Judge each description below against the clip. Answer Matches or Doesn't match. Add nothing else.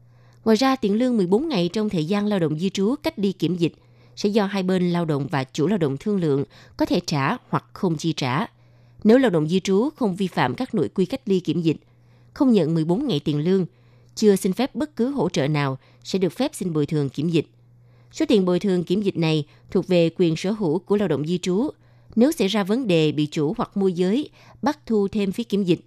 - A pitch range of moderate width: Doesn't match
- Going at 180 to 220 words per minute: Doesn't match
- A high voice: Doesn't match